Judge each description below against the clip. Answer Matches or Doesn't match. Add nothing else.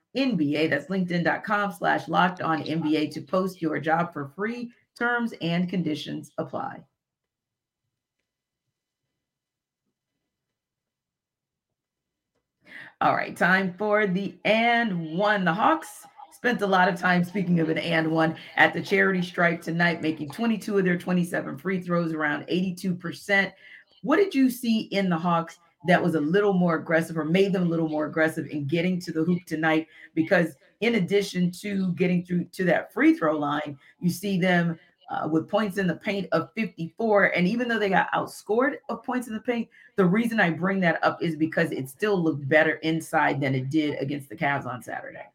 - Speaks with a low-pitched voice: Doesn't match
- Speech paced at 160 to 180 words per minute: Matches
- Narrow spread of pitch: Doesn't match